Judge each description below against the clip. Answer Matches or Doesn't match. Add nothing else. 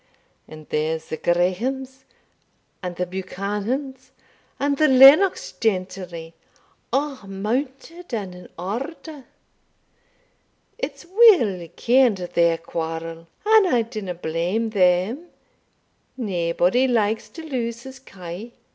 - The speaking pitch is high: Matches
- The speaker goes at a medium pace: Doesn't match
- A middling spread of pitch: Doesn't match